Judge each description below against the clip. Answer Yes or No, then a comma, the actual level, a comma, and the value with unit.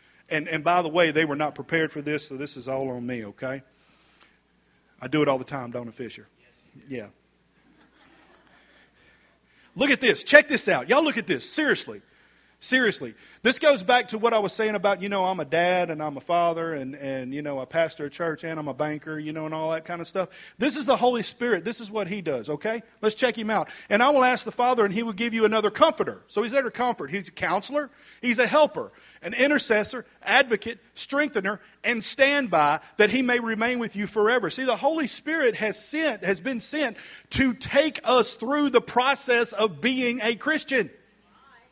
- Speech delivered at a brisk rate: Yes, fast, 215 wpm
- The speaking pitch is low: No, high, 215 Hz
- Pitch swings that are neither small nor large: No, wide, 7.6 semitones